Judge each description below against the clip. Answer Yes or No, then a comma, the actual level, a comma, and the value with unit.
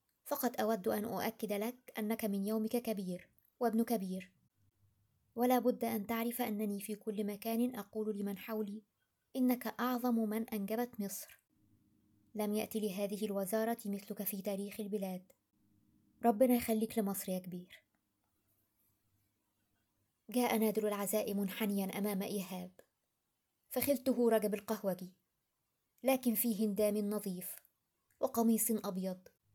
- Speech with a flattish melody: No, average, 3.6 semitones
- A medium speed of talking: Yes, average, 110 wpm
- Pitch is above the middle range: Yes, high, 210 Hz